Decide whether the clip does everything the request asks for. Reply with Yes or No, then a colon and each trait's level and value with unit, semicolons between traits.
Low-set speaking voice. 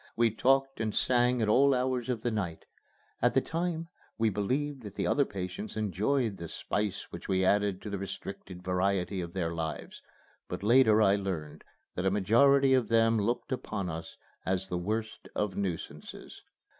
Yes: low, 105 Hz